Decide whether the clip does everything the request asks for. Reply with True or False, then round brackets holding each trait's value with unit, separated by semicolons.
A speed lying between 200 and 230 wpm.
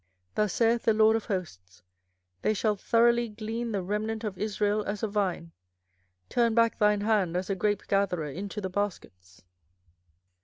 False (160 wpm)